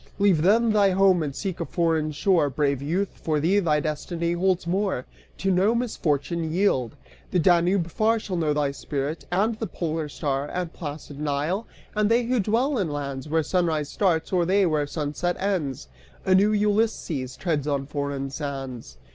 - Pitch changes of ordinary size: Yes, average, 4.9 semitones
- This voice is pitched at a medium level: Yes, medium, 170 Hz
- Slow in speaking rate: No, average, 175 wpm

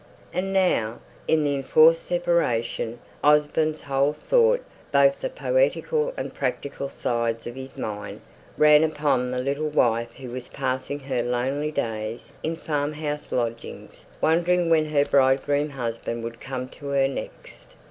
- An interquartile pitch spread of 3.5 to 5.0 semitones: Yes, average, 3.9 semitones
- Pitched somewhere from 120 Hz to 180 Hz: Yes, medium, 140 Hz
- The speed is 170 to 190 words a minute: No, average, 140 wpm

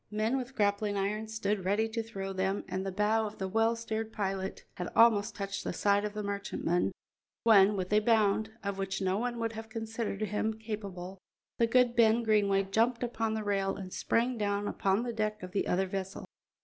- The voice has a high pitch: Yes, high, 210 Hz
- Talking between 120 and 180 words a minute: No, average, 200 wpm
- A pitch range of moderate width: No, narrow, 2.3 semitones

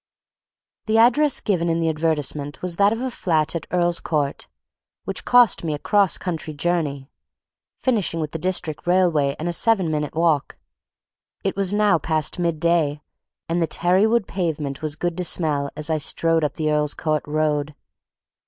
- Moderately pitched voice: Yes, medium, 165 Hz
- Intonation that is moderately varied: Yes, average, 3.1 semitones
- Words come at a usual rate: Yes, average, 175 wpm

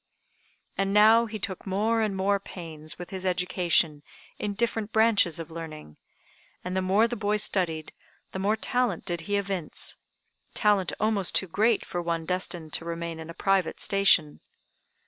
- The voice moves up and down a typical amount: Yes, average, 3.8 semitones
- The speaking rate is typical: Yes, average, 165 wpm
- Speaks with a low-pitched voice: No, high, 190 Hz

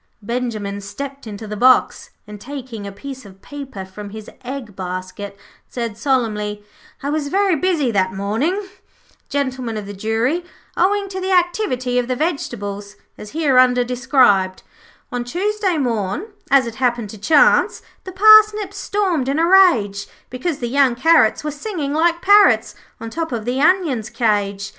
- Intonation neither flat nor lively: No, wide, 7.6 semitones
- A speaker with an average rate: Yes, average, 155 wpm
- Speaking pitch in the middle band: No, very high, 255 Hz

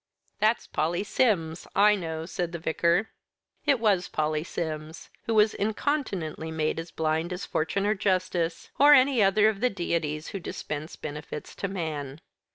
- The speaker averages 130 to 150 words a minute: No, average, 160 wpm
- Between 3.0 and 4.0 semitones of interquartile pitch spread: No, average, 4.7 semitones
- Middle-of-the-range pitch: Yes, medium, 175 Hz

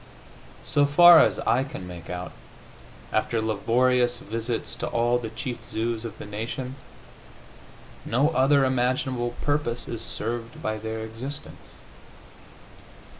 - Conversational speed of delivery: No, slow, 125 wpm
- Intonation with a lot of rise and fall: No, average, 2.7 semitones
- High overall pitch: No, low, 120 Hz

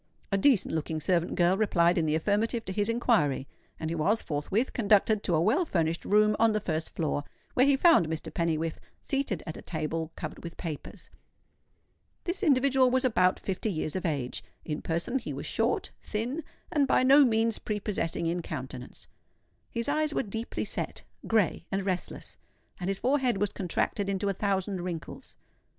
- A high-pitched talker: Yes, high, 195 Hz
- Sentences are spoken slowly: No, average, 175 wpm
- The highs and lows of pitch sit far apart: Yes, wide, 5.8 semitones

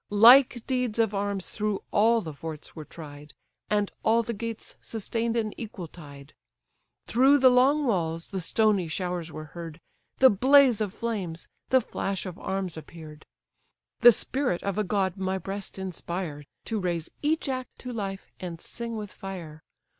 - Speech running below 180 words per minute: Yes, average, 160 wpm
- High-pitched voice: Yes, high, 200 Hz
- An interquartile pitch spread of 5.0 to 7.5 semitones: Yes, average, 5.3 semitones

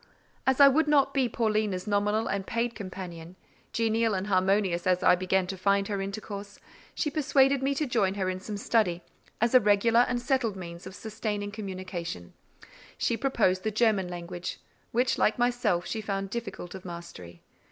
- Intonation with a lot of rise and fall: No, average, 3.9 semitones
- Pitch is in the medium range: No, high, 205 Hz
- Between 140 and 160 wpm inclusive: No, average, 175 wpm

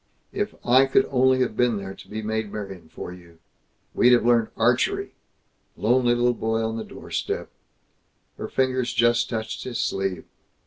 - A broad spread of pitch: No, average, 2.7 semitones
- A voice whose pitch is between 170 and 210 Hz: No, low, 115 Hz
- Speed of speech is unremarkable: Yes, average, 165 wpm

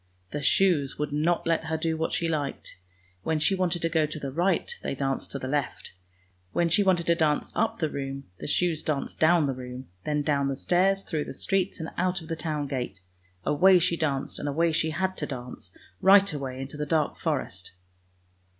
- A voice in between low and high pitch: Yes, medium, 155 Hz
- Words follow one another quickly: Yes, fast, 210 wpm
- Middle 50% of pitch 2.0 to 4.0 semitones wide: Yes, average, 3.3 semitones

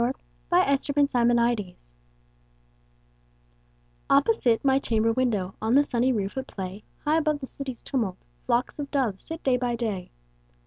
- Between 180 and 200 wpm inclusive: No, average, 150 wpm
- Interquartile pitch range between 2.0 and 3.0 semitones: No, average, 3.9 semitones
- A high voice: Yes, high, 245 Hz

